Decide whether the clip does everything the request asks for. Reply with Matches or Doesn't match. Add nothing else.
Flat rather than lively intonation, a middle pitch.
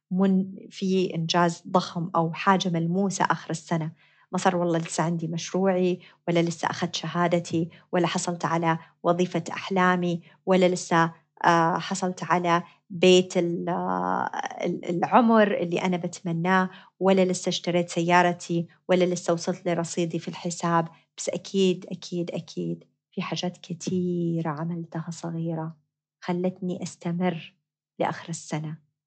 Matches